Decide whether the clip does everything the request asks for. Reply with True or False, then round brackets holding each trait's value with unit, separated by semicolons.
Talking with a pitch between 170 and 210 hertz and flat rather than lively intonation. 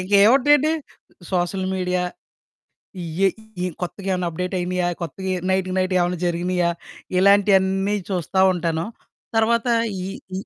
True (185 Hz; 1.8 semitones)